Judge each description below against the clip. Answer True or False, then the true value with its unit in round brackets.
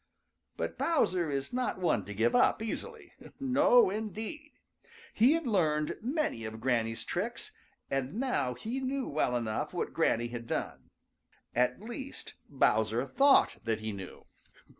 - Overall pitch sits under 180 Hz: False (185 Hz)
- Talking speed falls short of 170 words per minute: True (140 wpm)